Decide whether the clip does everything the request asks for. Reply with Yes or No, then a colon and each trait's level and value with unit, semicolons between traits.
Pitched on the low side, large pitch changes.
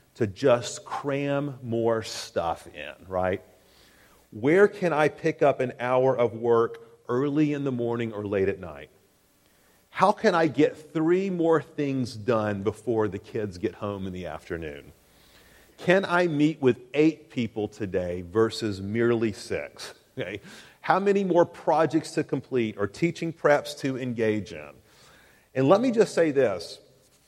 Yes: low, 125 Hz; wide, 6.0 semitones